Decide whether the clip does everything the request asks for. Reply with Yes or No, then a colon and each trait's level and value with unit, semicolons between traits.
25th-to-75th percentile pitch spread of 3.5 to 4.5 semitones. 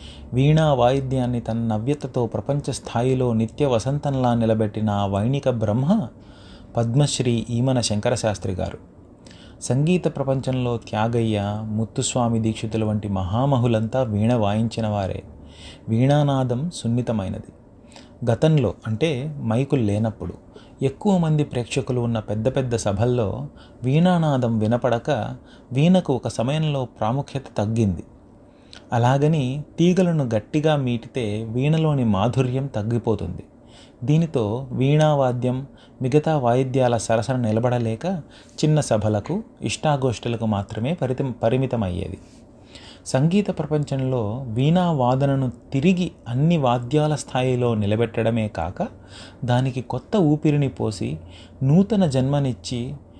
Yes: average, 3.9 semitones